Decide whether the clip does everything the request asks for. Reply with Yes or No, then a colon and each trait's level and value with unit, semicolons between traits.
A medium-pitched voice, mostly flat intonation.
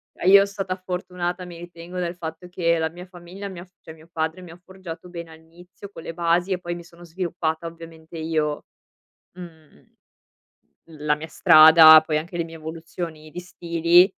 Yes: medium, 170 Hz; narrow, 1.8 semitones